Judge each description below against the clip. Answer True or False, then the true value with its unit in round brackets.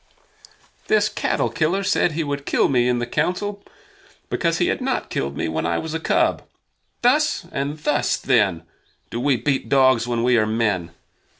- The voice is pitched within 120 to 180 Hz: True (135 Hz)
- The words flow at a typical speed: True (180 wpm)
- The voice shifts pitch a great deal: True (5.7 semitones)